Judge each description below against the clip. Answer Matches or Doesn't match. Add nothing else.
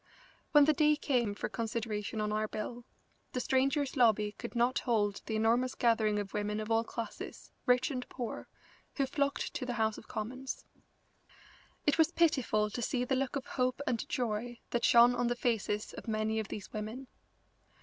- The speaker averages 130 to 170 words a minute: Doesn't match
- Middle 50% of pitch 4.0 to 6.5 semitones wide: Doesn't match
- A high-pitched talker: Matches